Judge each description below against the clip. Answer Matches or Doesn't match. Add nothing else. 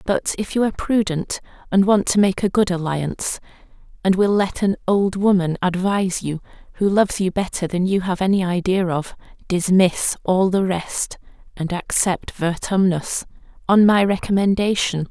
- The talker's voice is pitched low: Doesn't match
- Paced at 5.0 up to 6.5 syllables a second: Doesn't match